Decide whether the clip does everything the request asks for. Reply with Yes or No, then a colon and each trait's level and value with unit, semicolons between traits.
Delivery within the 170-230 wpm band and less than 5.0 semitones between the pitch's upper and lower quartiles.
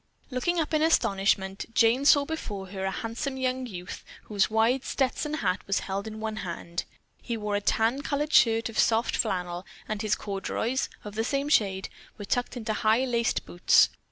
Yes: average, 180 wpm; average, 4.6 semitones